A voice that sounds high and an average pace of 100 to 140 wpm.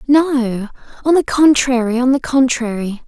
Yes: very high, 255 Hz; slow, 135 wpm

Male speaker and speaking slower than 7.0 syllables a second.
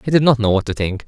No: male; 7.2 syllables/s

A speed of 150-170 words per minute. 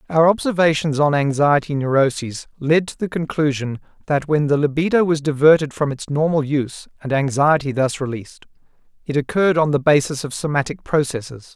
Yes: average, 160 wpm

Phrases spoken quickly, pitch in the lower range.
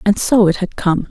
No: fast, 270 wpm; high, 195 Hz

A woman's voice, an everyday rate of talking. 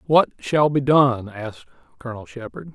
No: male; average, 155 wpm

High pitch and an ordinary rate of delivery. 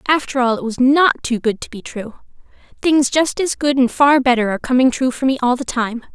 No: very high, 260 Hz; fast, 245 wpm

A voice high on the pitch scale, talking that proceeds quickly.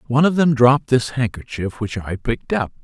No: low, 120 Hz; fast, 210 wpm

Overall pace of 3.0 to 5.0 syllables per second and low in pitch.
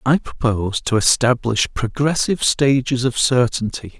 Yes: 4.6 syllables/s; low, 125 Hz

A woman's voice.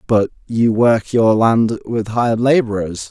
No: male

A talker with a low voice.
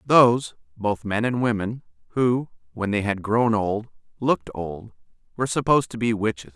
Yes: low, 110 Hz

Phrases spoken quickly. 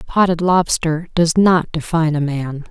No: average, 155 wpm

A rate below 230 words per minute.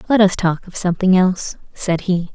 Yes: fast, 205 wpm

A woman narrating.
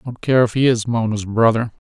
No: male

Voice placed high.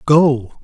No: low, 135 Hz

